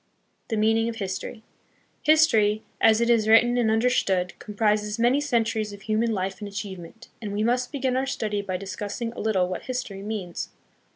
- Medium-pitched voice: No, high, 220 Hz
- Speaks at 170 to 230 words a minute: Yes, average, 175 wpm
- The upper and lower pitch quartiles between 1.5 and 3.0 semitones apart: Yes, narrow, 2.5 semitones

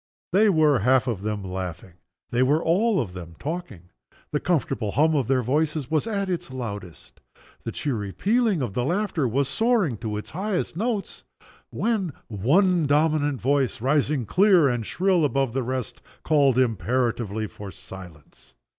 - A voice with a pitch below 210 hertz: Yes, low, 135 Hz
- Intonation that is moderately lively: No, wide, 7.3 semitones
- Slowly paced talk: No, average, 160 wpm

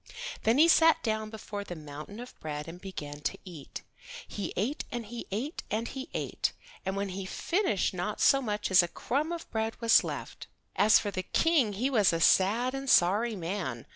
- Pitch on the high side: Yes, high, 210 Hz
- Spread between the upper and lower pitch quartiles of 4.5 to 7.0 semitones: Yes, average, 4.8 semitones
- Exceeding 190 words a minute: Yes, average, 200 wpm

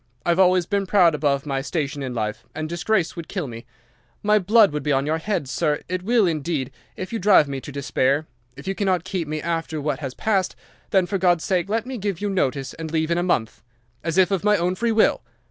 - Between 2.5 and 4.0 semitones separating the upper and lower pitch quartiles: No, average, 4.8 semitones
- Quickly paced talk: Yes, fast, 230 wpm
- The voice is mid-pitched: Yes, medium, 170 Hz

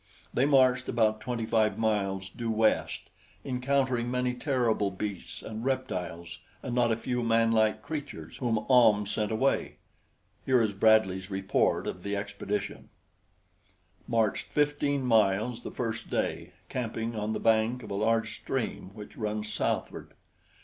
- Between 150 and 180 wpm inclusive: No, average, 140 wpm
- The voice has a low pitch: Yes, low, 110 Hz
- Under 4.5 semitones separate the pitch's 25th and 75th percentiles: Yes, average, 2.9 semitones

